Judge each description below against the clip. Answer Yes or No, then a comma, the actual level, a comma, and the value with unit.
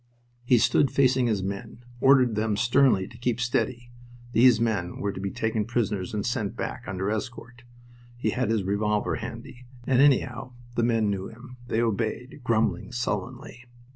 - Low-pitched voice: Yes, low, 115 Hz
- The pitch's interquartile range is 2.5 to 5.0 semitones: Yes, average, 2.8 semitones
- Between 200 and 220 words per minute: No, average, 170 wpm